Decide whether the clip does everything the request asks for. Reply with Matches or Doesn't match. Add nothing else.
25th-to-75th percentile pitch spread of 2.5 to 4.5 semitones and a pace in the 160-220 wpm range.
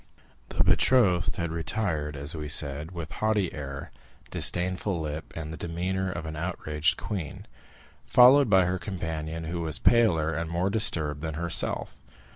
Doesn't match